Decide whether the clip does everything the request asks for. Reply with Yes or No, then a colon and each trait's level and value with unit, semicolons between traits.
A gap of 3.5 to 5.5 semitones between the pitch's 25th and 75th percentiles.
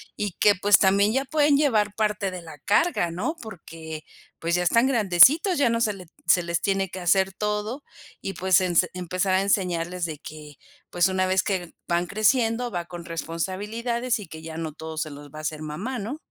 Yes: average, 4.1 semitones